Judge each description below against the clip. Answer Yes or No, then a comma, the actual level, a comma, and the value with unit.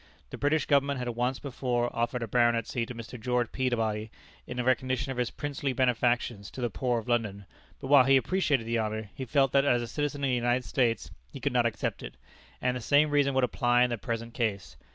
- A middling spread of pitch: No, narrow, 2.3 semitones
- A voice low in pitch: Yes, low, 125 Hz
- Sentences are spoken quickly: Yes, fast, 220 wpm